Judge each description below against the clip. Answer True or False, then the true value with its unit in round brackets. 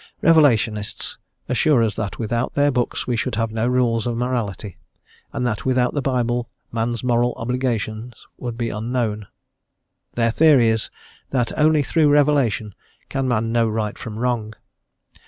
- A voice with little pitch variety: True (2.2 semitones)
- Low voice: True (120 Hz)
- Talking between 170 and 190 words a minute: False (150 wpm)